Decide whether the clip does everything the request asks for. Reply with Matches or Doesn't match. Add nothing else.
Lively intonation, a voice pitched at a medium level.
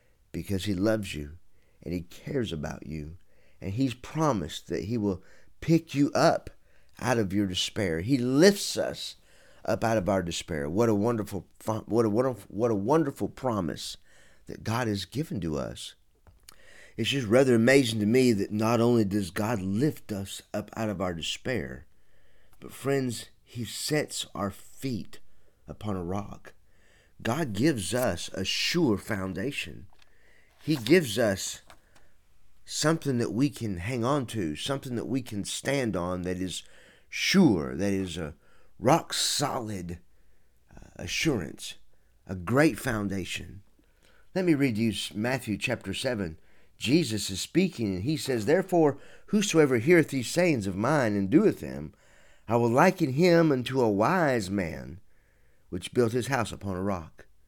Doesn't match